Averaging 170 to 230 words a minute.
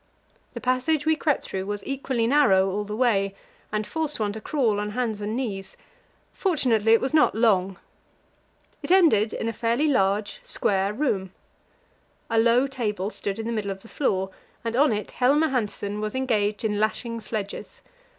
Yes: average, 175 wpm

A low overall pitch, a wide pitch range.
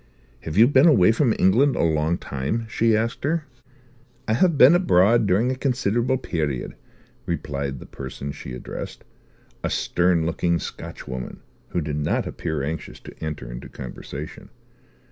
Yes: very low, 90 Hz; wide, 8.1 semitones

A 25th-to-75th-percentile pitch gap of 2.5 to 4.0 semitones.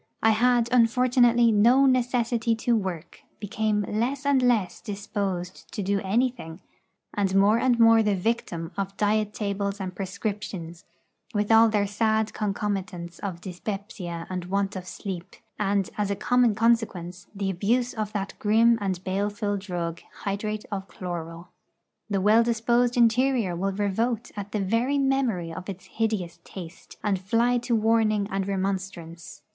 Yes: average, 3.2 semitones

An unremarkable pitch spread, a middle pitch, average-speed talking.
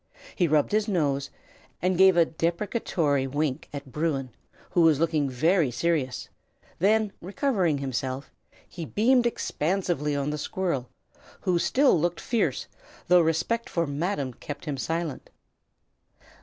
No: average, 4.6 semitones; medium, 165 Hz; slow, 130 wpm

